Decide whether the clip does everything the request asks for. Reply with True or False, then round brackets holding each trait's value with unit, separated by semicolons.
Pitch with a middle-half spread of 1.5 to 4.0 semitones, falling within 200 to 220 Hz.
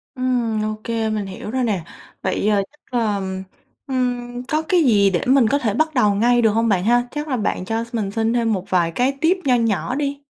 False (3.6 semitones; 230 Hz)